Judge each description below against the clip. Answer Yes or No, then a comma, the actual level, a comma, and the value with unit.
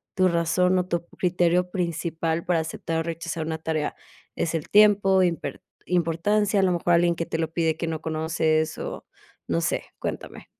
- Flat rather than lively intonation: Yes, narrow, 1.9 semitones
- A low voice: No, medium, 170 Hz